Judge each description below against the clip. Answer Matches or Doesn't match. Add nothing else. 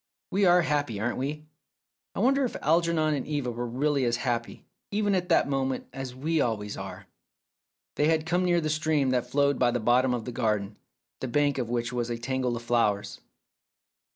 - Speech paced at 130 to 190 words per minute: Doesn't match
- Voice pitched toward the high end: Doesn't match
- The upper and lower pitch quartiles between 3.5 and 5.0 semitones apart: Matches